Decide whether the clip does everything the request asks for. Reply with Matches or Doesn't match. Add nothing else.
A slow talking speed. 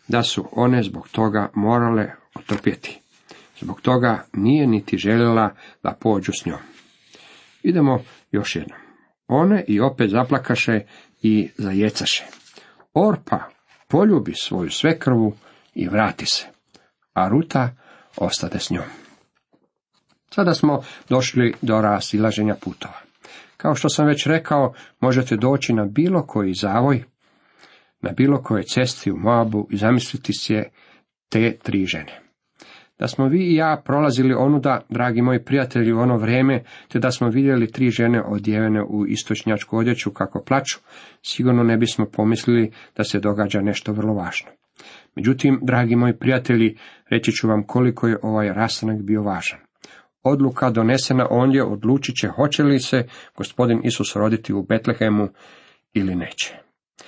Doesn't match